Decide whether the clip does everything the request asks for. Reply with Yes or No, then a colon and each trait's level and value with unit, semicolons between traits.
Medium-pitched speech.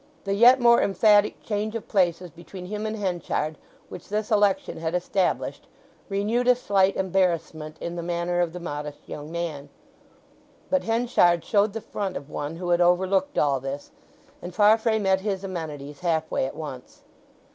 Yes: medium, 180 Hz